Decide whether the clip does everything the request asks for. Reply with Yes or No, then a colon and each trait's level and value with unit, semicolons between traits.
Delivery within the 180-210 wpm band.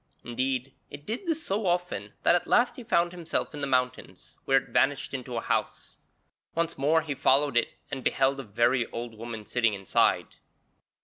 Yes: average, 185 wpm